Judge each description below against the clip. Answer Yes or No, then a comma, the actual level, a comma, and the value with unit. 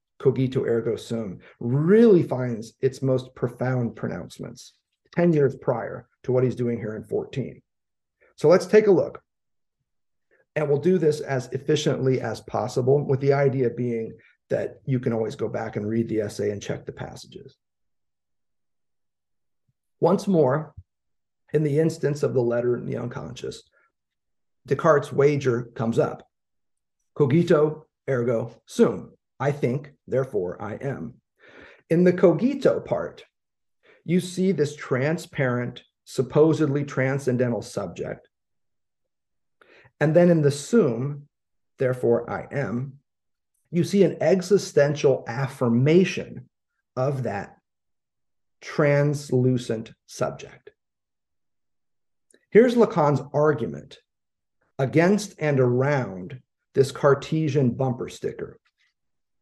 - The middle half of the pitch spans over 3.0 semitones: Yes, average, 3.9 semitones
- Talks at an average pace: No, slow, 110 wpm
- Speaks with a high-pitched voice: No, medium, 140 Hz